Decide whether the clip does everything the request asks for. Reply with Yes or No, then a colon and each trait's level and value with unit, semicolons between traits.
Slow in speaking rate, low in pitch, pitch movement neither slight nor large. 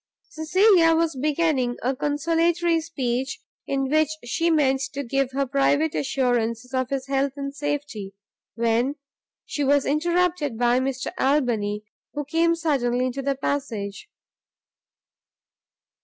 No: slow, 125 wpm; very high, 275 Hz; average, 3.6 semitones